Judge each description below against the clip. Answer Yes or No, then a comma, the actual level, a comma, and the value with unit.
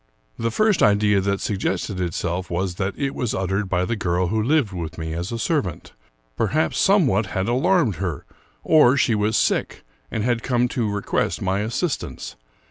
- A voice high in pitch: No, low, 105 Hz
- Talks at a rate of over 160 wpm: Yes, average, 180 wpm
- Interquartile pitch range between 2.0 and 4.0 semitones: No, average, 4.6 semitones